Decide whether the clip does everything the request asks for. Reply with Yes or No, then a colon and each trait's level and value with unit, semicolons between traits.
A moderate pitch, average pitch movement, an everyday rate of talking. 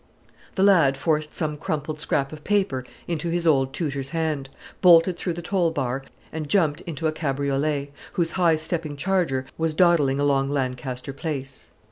Yes: medium, 155 Hz; average, 3.5 semitones; average, 160 wpm